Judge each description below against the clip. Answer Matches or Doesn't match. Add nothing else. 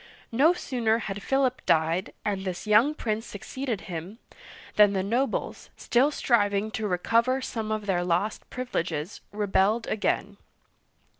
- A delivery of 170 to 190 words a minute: Doesn't match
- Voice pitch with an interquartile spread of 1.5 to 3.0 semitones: Doesn't match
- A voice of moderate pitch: Doesn't match